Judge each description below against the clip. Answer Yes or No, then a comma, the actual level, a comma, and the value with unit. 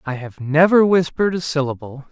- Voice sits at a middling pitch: Yes, medium, 155 Hz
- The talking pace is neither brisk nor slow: Yes, average, 170 wpm